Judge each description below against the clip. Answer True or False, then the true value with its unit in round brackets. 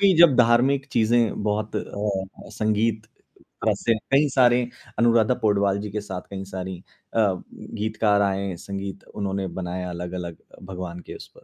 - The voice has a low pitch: True (105 Hz)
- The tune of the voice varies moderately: True (3.1 semitones)